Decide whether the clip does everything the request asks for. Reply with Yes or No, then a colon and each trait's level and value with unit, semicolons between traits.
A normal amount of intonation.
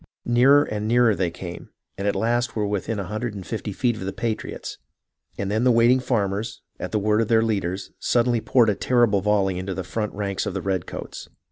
Yes: average, 3.1 semitones